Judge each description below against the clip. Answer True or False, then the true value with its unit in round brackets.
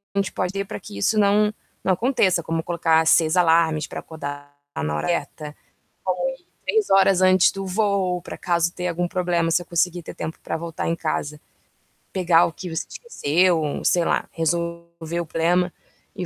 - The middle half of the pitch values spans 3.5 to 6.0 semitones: False (2.4 semitones)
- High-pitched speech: False (170 Hz)